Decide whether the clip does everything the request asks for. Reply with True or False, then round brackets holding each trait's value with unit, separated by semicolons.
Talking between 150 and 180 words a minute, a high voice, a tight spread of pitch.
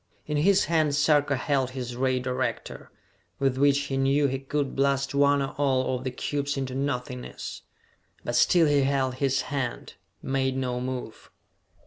False (160 wpm; 135 Hz; 1.7 semitones)